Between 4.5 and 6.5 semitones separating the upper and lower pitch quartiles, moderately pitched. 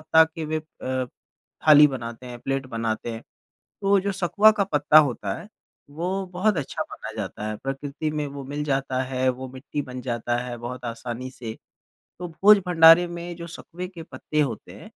Yes: average, 5.0 semitones; medium, 145 Hz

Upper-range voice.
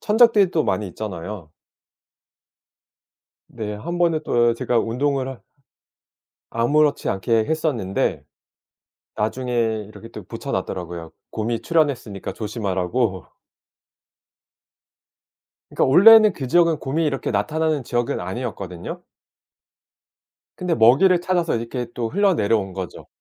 No: low, 120 Hz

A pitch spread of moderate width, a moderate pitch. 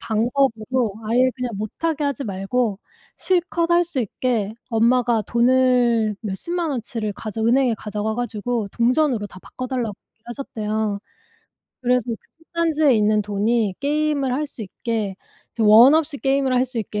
No: average, 3.9 semitones; high, 240 Hz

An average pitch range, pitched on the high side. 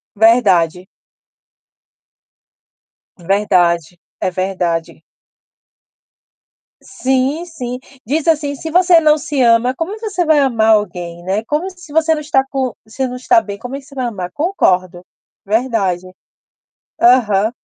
No: wide, 7.8 semitones; high, 245 Hz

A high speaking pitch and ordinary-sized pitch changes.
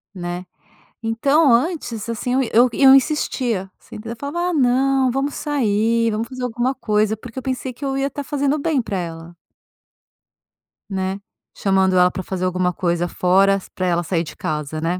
No: high, 225 Hz; wide, 6.5 semitones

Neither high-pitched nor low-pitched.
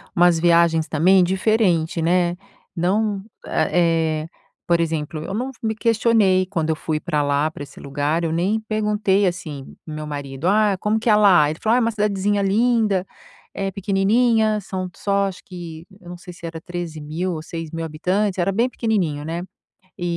Yes: medium, 180 Hz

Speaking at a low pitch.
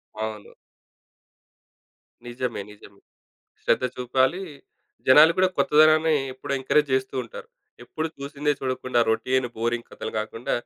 Yes: low, 130 Hz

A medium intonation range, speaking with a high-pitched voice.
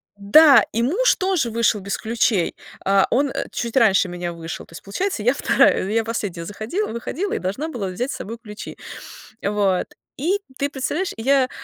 No: wide, 5.9 semitones; high, 230 Hz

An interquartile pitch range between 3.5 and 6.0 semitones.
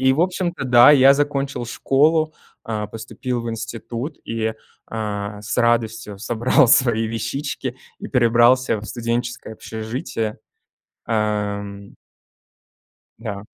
No: average, 3.1 semitones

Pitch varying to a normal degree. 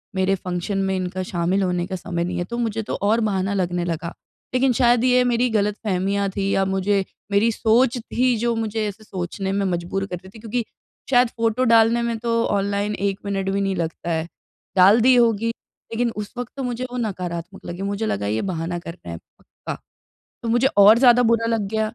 Yes: average, 3.8 semitones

